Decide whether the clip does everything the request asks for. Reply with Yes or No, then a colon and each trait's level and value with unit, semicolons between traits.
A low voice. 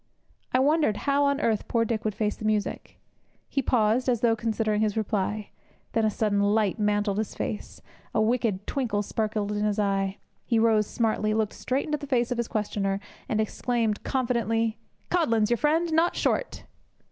No: high, 220 Hz